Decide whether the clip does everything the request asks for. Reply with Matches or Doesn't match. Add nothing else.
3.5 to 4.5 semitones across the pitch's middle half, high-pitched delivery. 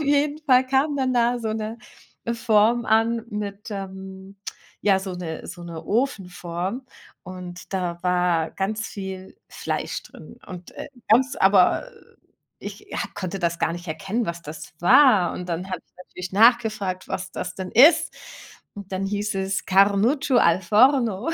Matches